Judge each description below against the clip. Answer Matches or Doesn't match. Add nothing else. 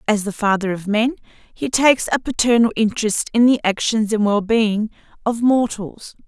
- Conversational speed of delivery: Matches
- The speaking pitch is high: Matches